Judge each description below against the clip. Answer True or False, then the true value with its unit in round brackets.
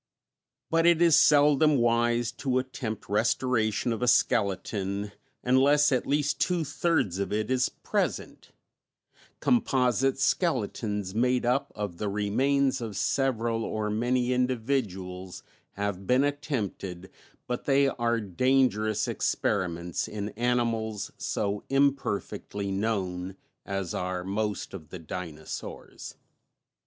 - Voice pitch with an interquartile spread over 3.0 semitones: True (4.7 semitones)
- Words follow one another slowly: True (115 wpm)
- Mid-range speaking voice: False (115 Hz)